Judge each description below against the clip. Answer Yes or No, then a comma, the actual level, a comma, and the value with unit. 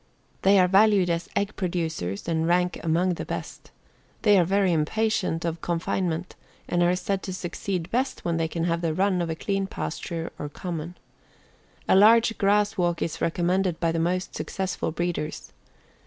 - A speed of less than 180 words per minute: Yes, average, 170 wpm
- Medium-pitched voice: Yes, medium, 175 Hz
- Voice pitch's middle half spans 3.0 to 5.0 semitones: No, narrow, 2.6 semitones